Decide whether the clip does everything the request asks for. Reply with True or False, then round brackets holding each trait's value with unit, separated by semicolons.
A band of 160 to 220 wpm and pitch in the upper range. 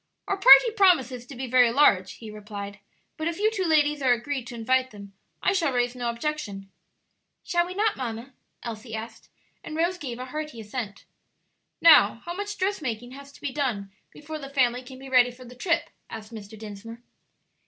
True (190 wpm; 255 Hz)